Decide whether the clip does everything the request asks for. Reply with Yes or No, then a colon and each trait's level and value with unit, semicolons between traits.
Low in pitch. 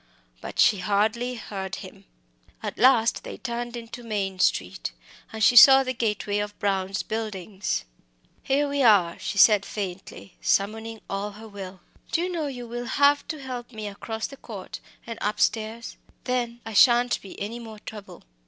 No: high, 220 Hz